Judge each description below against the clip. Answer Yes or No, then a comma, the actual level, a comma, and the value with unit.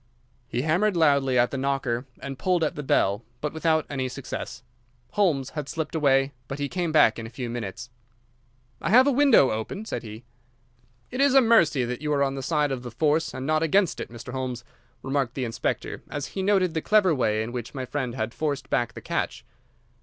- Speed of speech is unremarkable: No, fast, 215 wpm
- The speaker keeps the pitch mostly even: No, average, 4.4 semitones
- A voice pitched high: No, medium, 140 Hz